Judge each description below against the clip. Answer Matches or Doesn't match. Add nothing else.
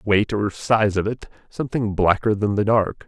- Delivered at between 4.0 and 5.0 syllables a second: Matches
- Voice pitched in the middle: Doesn't match